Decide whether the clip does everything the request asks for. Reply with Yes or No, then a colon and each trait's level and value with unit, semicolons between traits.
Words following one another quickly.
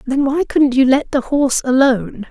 Yes: fast, 210 wpm